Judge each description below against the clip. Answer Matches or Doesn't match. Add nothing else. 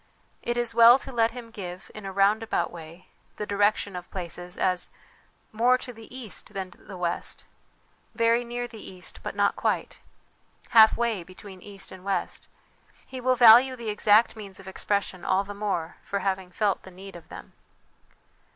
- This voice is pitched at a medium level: Doesn't match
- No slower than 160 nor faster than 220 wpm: Matches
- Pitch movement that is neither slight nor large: Matches